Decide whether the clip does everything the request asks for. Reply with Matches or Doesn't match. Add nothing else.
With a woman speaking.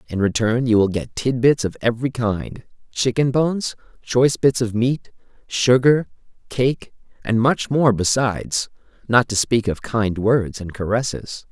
Doesn't match